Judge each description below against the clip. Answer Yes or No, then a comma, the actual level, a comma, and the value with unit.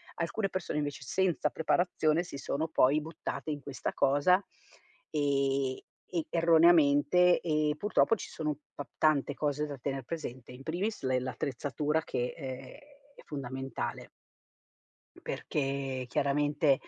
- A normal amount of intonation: Yes, average, 3.0 semitones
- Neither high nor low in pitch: Yes, medium, 145 Hz